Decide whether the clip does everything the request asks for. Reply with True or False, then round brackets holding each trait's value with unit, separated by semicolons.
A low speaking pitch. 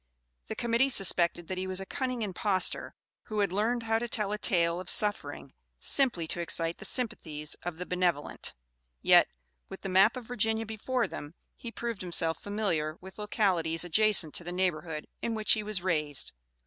False (190 Hz)